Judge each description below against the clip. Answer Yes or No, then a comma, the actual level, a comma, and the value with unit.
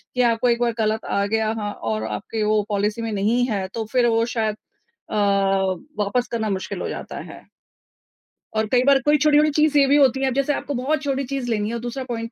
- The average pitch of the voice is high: Yes, high, 230 Hz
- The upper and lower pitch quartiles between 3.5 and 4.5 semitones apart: Yes, average, 4.2 semitones